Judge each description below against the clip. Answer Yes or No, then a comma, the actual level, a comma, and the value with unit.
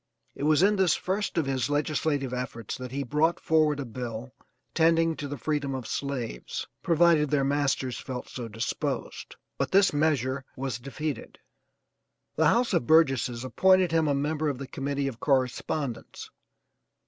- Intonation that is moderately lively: Yes, average, 3.6 semitones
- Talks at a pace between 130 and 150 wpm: No, average, 160 wpm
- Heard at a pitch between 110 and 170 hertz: Yes, medium, 140 Hz